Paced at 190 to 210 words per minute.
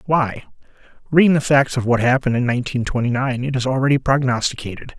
No: average, 180 wpm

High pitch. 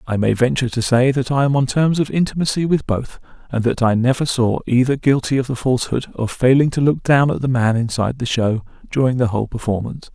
No: low, 125 Hz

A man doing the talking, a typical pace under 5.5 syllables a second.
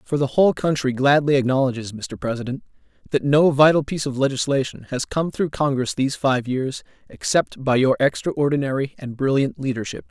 No: male; 5.6 syllables/s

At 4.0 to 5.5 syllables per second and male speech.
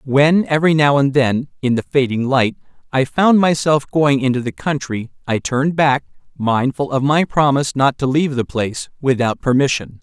Yes: 5.0 syllables/s; male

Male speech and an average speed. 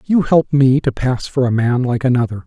No: male; fast, 245 wpm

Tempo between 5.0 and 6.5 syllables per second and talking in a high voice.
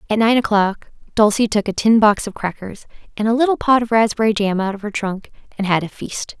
Yes: 5.7 syllables/s; high, 215 Hz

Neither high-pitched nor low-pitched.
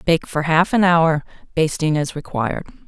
Yes: medium, 160 Hz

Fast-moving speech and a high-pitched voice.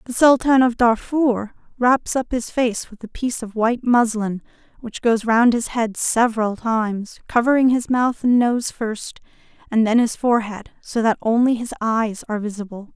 No: average, 175 wpm; high, 230 Hz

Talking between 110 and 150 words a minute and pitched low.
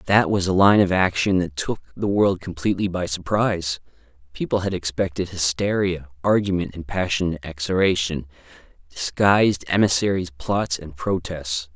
Yes: slow, 135 wpm; very low, 90 Hz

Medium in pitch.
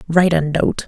Yes: medium, 165 Hz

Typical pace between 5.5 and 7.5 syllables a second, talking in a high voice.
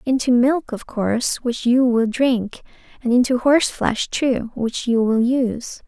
No: 4.2 syllables/s; high, 245 Hz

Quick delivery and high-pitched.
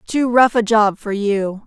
Yes: fast, 215 wpm; high, 220 Hz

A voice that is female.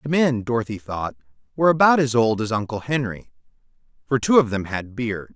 No: male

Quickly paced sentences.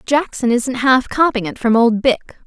No: average, 195 wpm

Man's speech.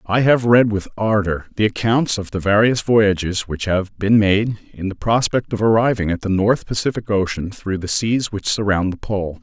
Yes: male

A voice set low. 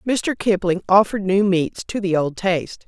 No: high, 190 Hz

